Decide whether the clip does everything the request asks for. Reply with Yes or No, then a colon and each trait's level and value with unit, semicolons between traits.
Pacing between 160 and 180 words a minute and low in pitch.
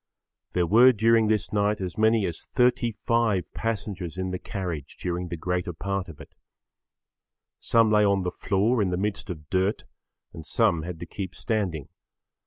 Yes: average, 170 wpm; very low, 95 Hz